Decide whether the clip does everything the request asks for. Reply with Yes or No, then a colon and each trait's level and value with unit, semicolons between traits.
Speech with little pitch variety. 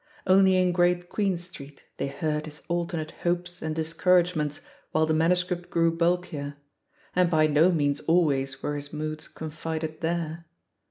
Yes: narrow, 2.3 semitones